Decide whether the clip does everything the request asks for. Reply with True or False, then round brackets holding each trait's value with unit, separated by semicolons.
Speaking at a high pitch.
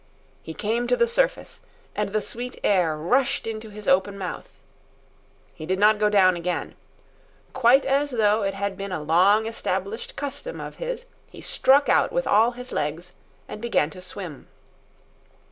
True (210 Hz)